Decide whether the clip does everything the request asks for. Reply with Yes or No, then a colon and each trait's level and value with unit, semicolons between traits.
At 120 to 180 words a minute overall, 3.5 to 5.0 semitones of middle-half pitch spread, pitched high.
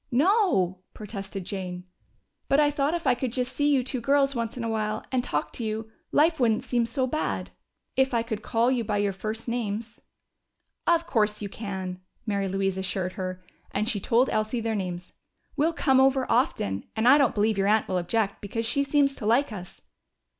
No: fast, 205 wpm; average, 4.7 semitones; high, 225 Hz